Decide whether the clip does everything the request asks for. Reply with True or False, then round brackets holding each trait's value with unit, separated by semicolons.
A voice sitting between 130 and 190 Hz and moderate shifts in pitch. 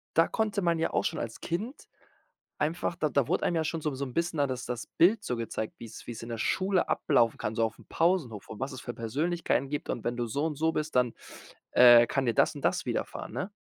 False (140 Hz; 6.0 semitones)